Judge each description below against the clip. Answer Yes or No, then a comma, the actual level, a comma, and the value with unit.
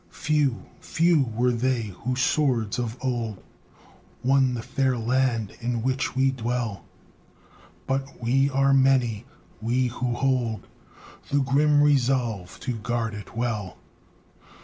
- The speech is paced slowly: Yes, slow, 125 wpm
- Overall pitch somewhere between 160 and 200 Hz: No, low, 125 Hz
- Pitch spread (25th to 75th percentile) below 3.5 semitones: Yes, average, 2.7 semitones